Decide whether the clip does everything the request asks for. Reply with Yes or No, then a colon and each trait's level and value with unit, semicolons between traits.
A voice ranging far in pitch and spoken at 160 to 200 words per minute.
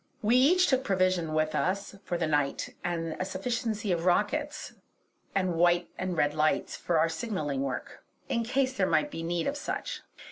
Yes: wide, 6.0 semitones; average, 180 wpm